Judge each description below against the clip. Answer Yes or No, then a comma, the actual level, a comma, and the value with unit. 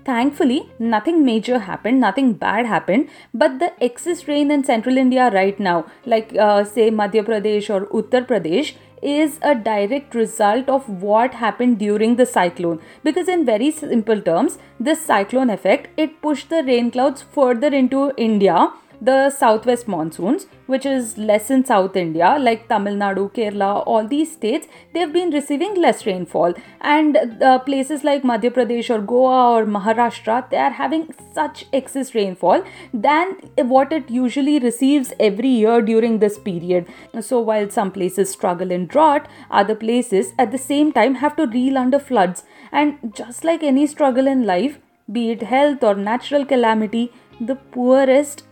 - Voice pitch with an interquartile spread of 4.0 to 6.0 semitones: Yes, average, 4.7 semitones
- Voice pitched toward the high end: Yes, high, 245 Hz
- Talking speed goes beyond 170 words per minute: No, average, 160 wpm